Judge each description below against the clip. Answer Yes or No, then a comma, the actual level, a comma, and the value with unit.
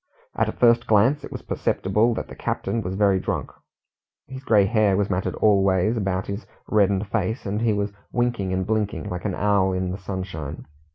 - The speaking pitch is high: No, low, 100 Hz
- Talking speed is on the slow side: No, average, 195 wpm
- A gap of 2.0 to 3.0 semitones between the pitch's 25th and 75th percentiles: Yes, average, 2.7 semitones